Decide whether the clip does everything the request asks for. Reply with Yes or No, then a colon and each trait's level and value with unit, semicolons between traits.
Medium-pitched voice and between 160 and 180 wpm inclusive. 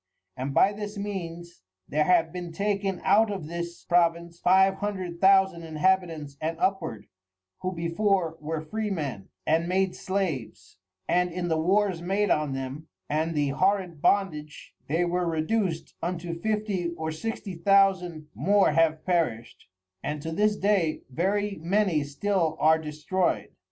No: medium, 175 Hz; average, 140 wpm